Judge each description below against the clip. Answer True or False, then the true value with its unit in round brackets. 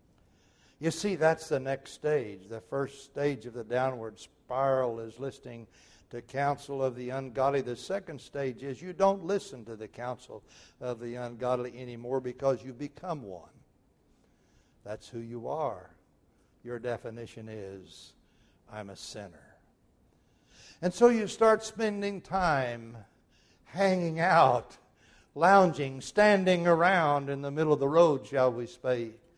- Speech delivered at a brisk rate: False (140 wpm)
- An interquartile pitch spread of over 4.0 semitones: True (5.2 semitones)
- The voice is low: True (130 Hz)